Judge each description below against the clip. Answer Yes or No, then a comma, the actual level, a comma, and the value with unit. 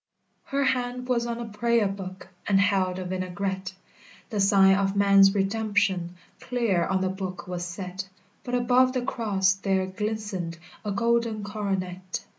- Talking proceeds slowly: No, average, 150 wpm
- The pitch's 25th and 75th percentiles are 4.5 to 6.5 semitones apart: No, average, 3.2 semitones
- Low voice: No, high, 195 Hz